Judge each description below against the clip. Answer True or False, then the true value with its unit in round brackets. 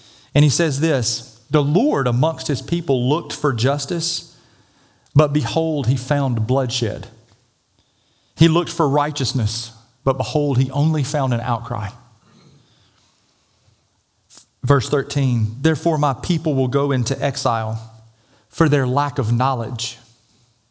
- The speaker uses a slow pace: True (120 wpm)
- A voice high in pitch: False (130 Hz)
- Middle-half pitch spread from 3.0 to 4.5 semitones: True (4.2 semitones)